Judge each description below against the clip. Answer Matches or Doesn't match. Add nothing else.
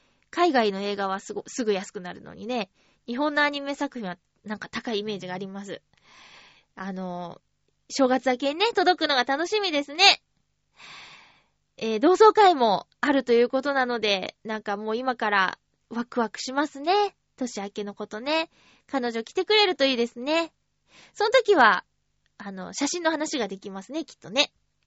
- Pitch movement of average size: Doesn't match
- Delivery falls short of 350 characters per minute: Matches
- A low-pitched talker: Doesn't match